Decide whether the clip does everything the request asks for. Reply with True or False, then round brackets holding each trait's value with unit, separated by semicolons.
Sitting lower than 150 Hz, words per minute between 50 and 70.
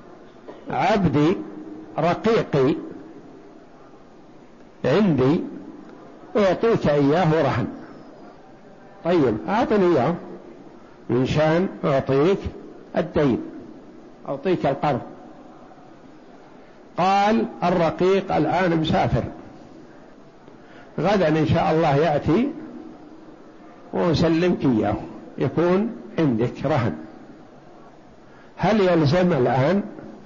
False (175 Hz; 65 wpm)